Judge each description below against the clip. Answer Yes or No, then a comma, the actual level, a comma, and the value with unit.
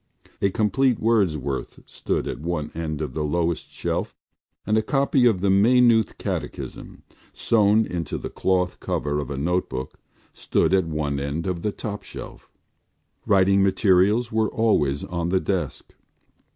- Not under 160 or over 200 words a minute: No, average, 150 wpm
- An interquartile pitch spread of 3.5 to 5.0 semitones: No, wide, 5.5 semitones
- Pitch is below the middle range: Yes, very low, 95 Hz